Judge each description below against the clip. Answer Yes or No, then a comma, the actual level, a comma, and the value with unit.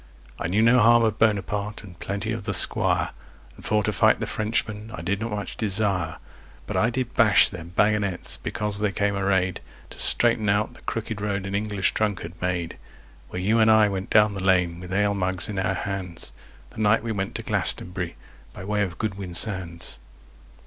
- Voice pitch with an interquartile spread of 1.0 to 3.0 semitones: Yes, narrow, 2.5 semitones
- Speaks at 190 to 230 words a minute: Yes, average, 195 wpm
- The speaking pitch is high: No, low, 100 Hz